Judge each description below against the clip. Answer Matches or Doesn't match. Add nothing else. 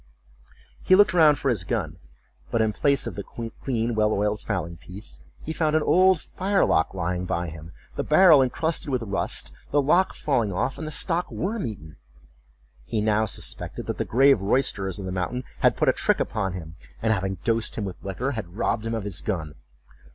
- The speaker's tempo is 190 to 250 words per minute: Matches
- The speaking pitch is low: Matches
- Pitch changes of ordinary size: Doesn't match